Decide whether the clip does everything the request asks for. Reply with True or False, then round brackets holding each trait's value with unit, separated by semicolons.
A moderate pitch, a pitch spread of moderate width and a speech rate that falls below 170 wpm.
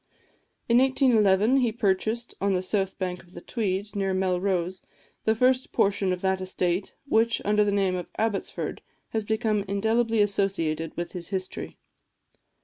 False (200 Hz; 3.0 semitones; 150 wpm)